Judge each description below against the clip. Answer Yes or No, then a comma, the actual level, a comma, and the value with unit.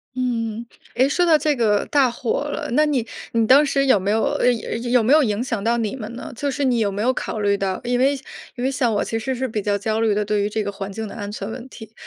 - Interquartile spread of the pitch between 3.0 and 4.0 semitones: Yes, average, 3.7 semitones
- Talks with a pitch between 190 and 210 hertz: No, high, 230 Hz